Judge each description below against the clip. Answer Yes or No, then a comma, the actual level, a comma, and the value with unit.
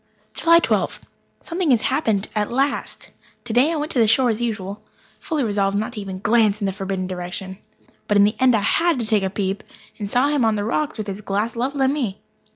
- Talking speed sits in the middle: No, fast, 225 wpm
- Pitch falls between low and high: No, high, 220 Hz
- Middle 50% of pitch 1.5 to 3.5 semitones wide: No, average, 4.6 semitones